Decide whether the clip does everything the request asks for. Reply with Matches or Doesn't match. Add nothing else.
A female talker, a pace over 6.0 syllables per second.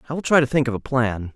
Doesn't match